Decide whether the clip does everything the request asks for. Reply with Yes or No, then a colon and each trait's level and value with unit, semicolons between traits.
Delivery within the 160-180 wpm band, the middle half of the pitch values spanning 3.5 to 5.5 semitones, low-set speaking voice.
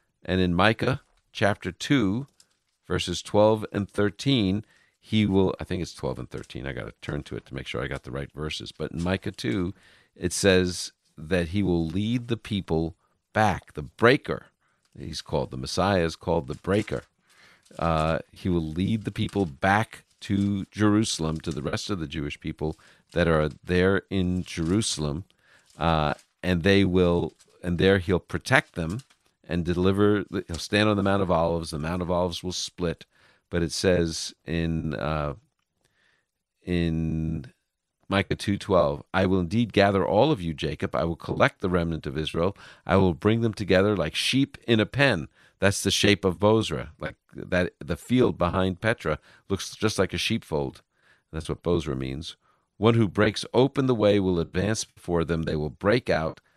Yes: average, 170 wpm; average, 4.1 semitones; very low, 90 Hz